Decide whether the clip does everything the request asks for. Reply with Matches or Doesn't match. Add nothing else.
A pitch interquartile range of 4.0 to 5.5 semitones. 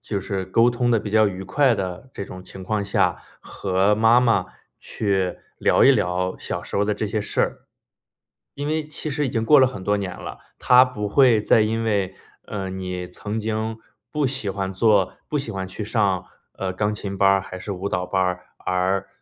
Doesn't match